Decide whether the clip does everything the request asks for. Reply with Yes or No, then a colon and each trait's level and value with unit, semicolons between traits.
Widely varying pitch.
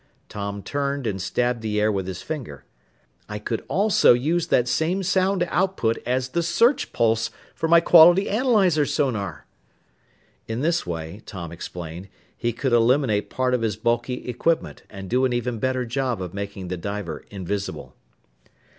Yes: wide, 7.3 semitones